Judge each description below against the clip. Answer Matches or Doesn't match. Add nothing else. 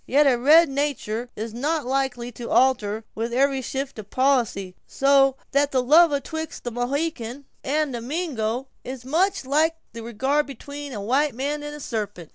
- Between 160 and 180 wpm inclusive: Matches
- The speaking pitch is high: Matches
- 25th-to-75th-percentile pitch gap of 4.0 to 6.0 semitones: Doesn't match